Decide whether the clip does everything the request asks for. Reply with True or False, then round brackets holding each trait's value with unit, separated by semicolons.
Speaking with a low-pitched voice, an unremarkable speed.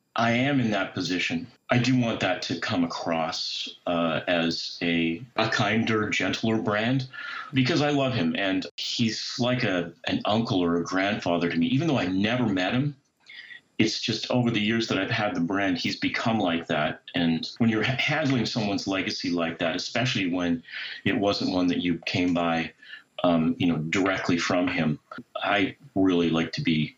True (105 Hz; 180 wpm)